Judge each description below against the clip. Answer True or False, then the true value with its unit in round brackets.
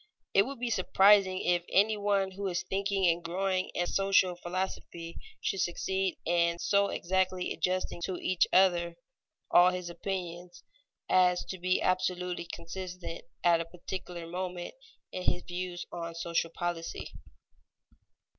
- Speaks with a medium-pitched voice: True (180 Hz)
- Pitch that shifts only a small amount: True (1.6 semitones)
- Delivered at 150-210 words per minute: False (135 wpm)